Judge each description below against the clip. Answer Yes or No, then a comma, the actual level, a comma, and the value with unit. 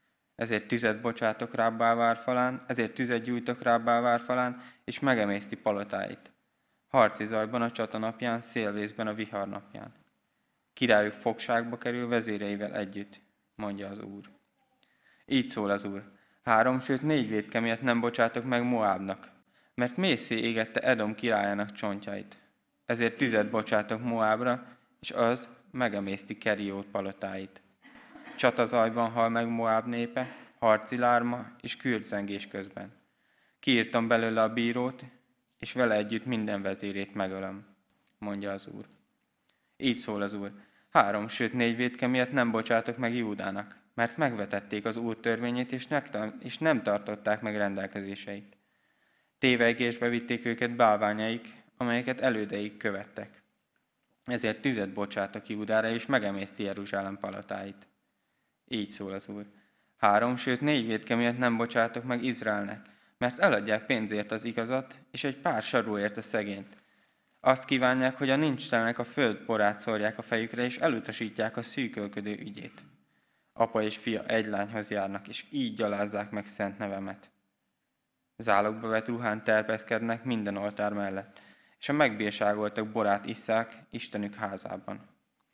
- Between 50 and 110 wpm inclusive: No, average, 130 wpm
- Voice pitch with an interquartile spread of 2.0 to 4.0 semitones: Yes, average, 2.7 semitones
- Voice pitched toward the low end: Yes, low, 110 Hz